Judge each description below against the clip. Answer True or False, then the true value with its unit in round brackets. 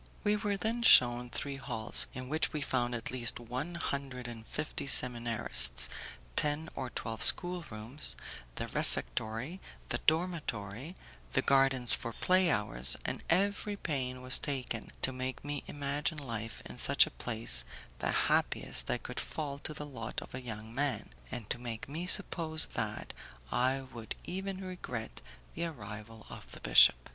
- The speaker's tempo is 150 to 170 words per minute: True (155 wpm)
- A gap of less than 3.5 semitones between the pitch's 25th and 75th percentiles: False (5.2 semitones)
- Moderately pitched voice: False (130 Hz)